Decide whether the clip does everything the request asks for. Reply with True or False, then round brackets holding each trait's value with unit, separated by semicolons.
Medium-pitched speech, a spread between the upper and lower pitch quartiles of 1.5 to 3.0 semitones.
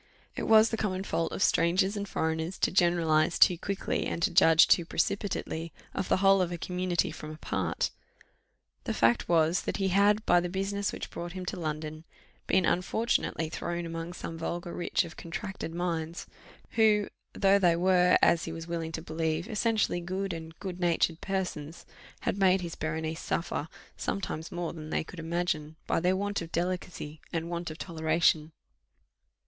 True (175 Hz; 2.7 semitones)